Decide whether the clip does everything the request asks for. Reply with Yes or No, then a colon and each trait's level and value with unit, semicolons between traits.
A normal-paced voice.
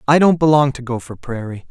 No: fast, 210 wpm